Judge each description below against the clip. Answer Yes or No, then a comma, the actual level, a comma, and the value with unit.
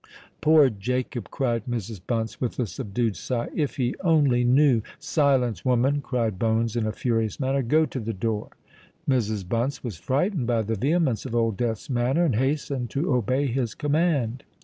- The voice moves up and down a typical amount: Yes, average, 3.4 semitones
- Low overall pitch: Yes, low, 125 Hz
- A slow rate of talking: No, average, 170 wpm